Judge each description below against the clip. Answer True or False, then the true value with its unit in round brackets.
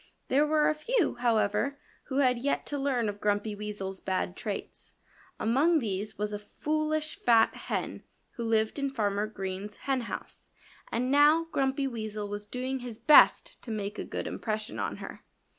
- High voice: True (230 Hz)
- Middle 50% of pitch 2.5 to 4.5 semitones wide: False (4.9 semitones)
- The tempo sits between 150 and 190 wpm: True (165 wpm)